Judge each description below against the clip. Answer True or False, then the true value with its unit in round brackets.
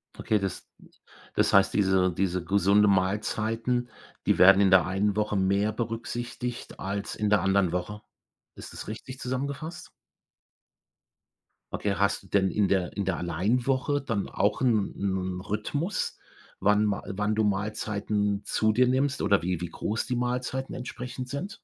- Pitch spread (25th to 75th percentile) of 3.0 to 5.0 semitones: True (4.0 semitones)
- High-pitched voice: False (105 Hz)